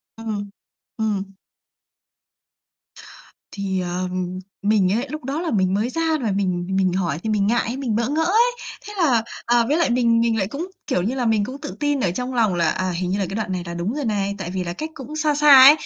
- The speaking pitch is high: Yes, high, 220 Hz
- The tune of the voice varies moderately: No, wide, 5.9 semitones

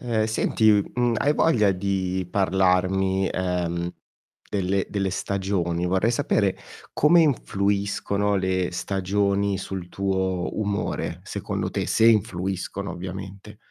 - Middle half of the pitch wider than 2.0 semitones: No, narrow, 1.7 semitones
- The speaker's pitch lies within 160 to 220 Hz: No, very low, 95 Hz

